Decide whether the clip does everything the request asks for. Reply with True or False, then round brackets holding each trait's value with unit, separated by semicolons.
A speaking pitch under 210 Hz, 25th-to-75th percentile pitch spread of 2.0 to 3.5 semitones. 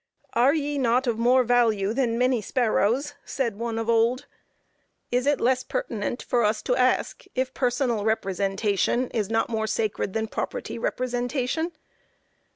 False (240 Hz; 2.6 semitones)